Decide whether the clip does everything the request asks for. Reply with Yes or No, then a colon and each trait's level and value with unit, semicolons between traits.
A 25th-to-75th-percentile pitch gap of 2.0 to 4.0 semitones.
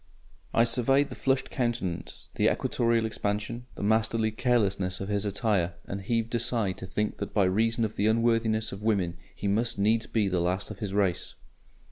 Yes: average, 2.7 semitones